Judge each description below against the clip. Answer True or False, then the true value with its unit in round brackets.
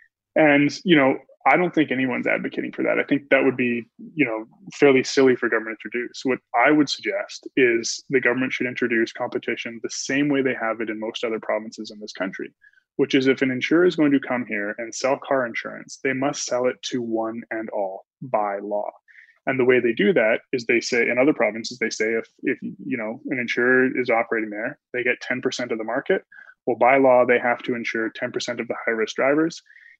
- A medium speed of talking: False (225 wpm)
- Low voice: True (125 Hz)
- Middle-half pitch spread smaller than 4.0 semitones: True (3.3 semitones)